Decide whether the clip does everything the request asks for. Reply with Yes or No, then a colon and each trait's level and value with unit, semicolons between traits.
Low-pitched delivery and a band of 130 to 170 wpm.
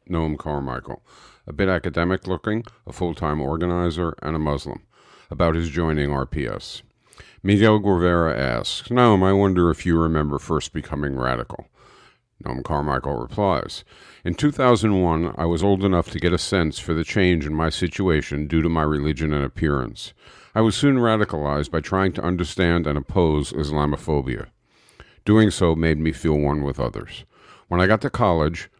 Yes: very low, 80 Hz; average, 165 wpm